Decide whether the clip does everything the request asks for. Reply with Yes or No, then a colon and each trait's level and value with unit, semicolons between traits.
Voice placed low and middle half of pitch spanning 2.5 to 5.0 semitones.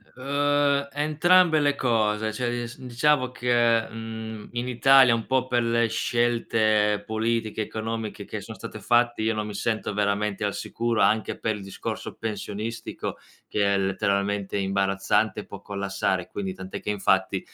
Yes: low, 110 Hz; average, 2.9 semitones